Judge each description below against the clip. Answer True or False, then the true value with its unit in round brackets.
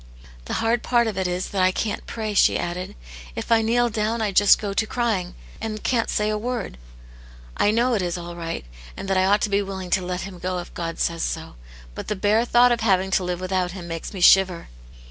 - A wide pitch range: False (3.5 semitones)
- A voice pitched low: False (195 Hz)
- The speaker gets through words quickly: True (240 wpm)